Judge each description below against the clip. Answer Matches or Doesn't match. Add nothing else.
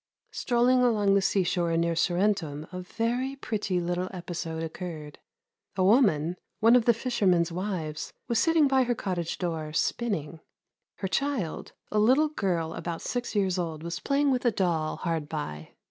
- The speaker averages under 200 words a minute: Matches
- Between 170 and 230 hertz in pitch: Matches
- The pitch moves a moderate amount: Doesn't match